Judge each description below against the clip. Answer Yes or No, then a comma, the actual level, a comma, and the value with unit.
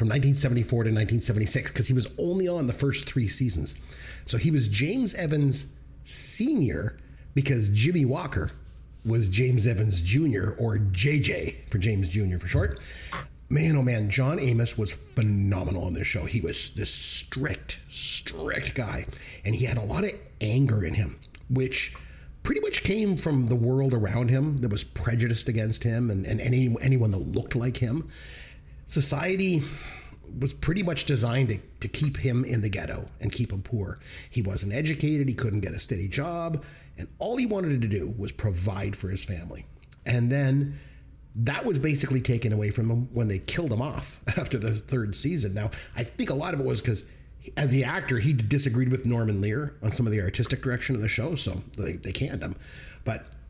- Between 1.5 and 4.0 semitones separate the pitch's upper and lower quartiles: No, average, 5.0 semitones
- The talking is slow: No, average, 185 wpm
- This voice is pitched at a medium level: No, low, 120 Hz